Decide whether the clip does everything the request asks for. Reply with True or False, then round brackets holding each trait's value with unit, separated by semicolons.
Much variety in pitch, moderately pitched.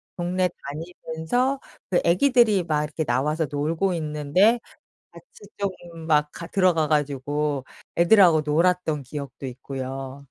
False (3.8 semitones; 155 Hz)